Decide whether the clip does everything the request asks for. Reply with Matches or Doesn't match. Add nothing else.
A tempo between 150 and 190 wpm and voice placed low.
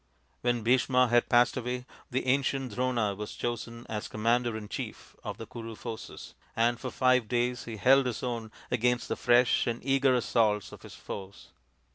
Matches